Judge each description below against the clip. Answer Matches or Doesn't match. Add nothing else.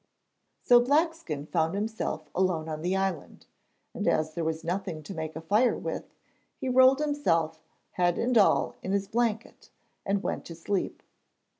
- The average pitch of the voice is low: Doesn't match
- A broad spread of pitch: Matches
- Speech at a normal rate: Matches